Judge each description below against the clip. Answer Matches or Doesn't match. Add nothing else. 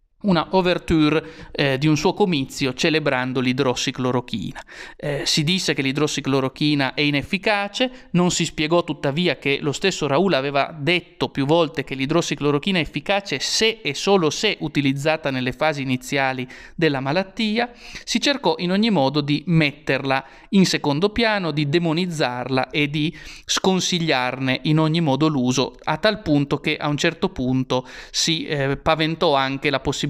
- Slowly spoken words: Doesn't match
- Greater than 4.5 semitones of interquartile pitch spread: Doesn't match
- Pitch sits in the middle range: Matches